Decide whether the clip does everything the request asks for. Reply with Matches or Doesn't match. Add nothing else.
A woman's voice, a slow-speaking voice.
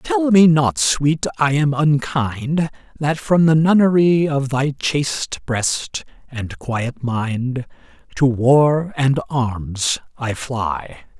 Doesn't match